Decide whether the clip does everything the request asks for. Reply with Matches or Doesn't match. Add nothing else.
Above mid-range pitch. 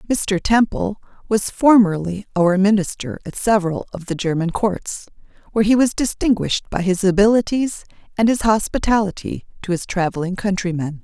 Matches